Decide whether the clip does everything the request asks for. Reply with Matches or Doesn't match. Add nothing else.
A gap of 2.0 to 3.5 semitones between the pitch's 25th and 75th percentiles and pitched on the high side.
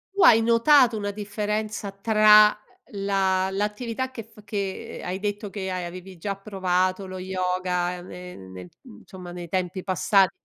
Matches